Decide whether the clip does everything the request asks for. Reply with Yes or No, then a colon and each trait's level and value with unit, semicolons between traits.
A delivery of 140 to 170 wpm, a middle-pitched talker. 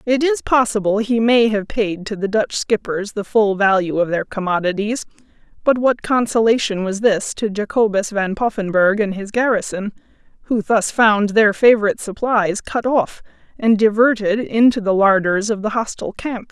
No: average, 165 wpm; high, 210 Hz